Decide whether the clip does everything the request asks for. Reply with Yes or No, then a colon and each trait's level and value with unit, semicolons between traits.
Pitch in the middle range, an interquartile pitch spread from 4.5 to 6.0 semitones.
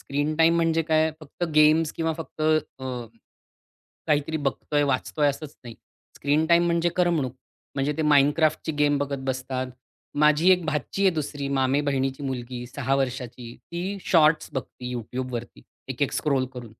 No: medium, 145 Hz; average, 3.2 semitones